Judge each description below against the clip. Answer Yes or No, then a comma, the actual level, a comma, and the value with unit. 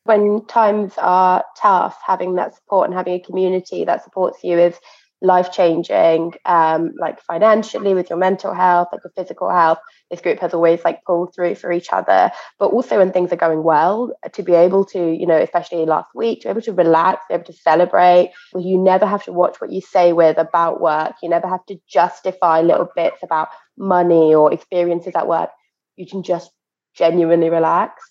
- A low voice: No, medium, 180 Hz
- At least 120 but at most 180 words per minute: No, average, 195 wpm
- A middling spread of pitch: No, narrow, 1.7 semitones